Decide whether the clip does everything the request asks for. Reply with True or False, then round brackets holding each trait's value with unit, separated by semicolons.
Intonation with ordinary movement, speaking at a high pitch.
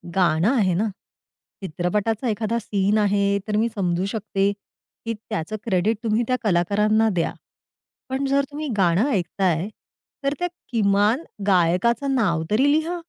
True (3.9 semitones; 210 Hz)